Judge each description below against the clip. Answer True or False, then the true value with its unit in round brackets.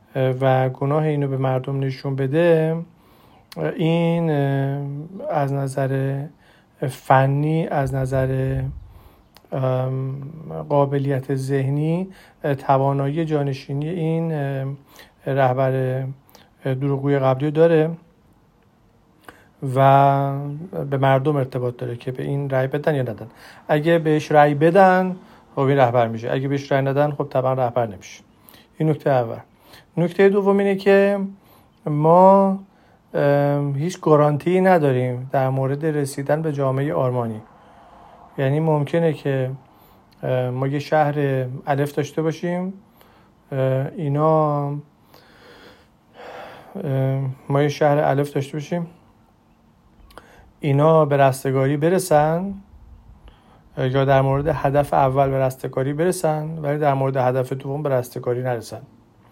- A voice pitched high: False (140 Hz)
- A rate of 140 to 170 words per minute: False (105 wpm)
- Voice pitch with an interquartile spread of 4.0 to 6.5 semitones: False (2.7 semitones)